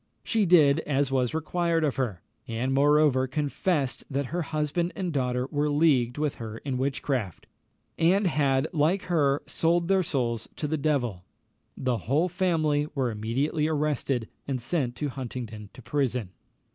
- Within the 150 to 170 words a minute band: Yes, average, 155 wpm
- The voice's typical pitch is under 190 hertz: Yes, medium, 140 Hz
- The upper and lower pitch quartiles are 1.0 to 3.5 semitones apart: No, average, 3.9 semitones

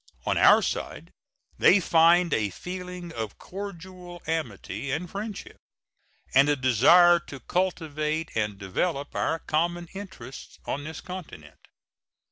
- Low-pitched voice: No, medium, 165 Hz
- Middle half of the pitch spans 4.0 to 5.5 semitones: Yes, average, 4.6 semitones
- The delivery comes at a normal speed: No, slow, 120 wpm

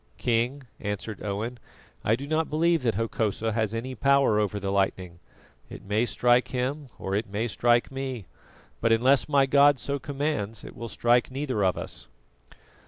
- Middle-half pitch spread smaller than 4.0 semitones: No, average, 4.5 semitones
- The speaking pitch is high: No, low, 120 Hz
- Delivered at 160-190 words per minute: Yes, average, 170 wpm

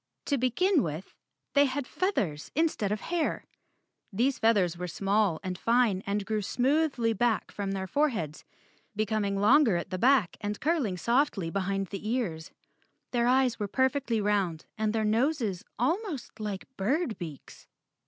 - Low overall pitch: No, high, 220 Hz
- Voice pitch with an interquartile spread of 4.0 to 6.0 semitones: Yes, average, 5.2 semitones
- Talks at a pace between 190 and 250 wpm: No, average, 150 wpm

